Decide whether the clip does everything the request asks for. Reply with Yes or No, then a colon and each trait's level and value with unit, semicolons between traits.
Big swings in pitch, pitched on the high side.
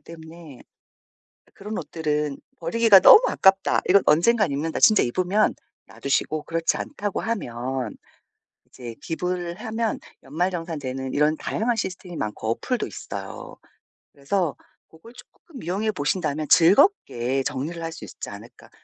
No: wide, 5.9 semitones; medium, 165 Hz